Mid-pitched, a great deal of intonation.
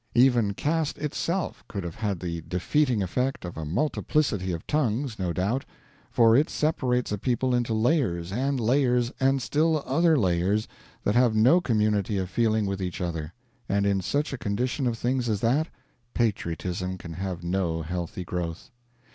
No: low, 110 Hz; wide, 6.2 semitones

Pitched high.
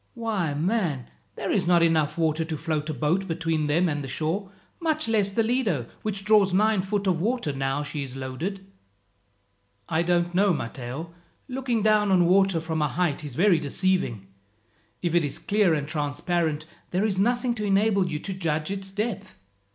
No: medium, 175 Hz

